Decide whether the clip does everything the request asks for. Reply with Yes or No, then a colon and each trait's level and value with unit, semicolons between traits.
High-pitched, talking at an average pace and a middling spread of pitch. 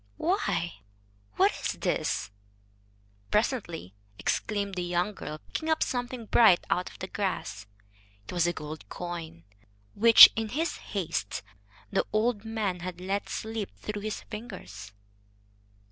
No: high, 195 Hz; slow, 130 wpm; average, 4.5 semitones